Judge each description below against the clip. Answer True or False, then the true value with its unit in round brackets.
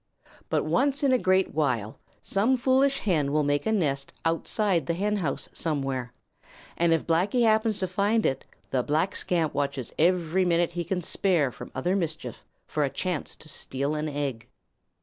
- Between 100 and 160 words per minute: False (170 wpm)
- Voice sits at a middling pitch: True (170 Hz)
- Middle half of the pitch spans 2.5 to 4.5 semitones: False (5.4 semitones)